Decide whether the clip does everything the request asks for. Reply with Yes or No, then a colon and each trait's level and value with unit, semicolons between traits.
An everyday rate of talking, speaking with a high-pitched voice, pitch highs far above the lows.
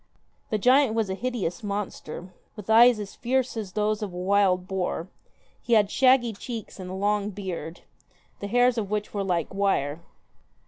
No: average, 175 wpm; high, 205 Hz; average, 3.2 semitones